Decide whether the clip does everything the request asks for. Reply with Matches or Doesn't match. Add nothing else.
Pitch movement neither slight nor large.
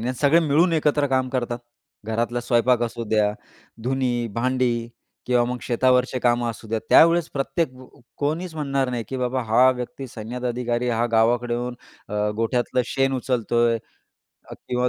Doesn't match